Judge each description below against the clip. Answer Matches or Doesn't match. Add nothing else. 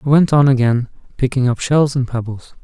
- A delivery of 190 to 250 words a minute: Matches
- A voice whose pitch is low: Matches